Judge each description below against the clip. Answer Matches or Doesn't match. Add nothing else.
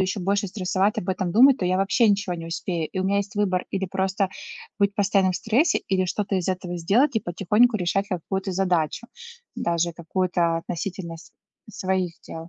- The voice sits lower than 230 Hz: Matches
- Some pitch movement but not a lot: Doesn't match